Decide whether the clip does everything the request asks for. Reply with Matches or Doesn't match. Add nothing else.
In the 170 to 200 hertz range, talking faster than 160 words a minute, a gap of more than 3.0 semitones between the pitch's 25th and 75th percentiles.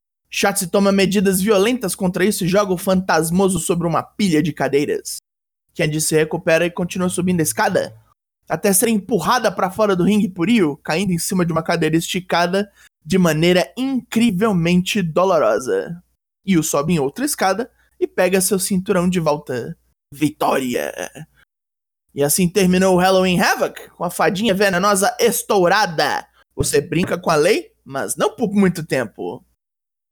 Doesn't match